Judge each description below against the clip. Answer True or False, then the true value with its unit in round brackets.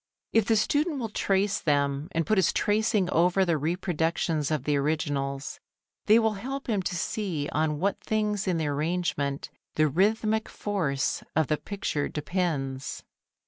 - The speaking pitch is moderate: True (175 Hz)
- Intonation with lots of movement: True (5.8 semitones)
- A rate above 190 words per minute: False (155 wpm)